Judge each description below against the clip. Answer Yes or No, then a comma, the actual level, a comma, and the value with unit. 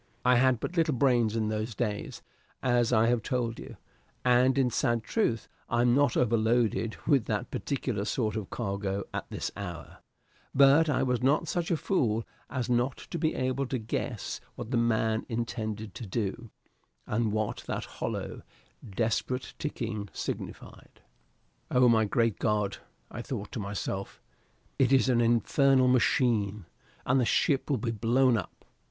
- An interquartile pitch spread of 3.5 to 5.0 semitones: No, average, 3.0 semitones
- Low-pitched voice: Yes, low, 120 Hz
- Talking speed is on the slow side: No, average, 160 wpm